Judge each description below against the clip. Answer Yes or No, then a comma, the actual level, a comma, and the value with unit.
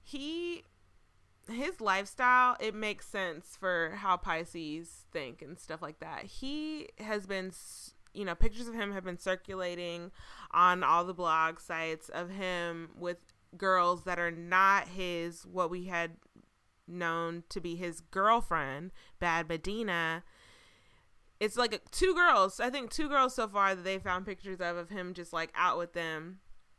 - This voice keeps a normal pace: Yes, average, 155 wpm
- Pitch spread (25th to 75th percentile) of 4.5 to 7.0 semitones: No, average, 3.5 semitones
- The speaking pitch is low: No, medium, 180 Hz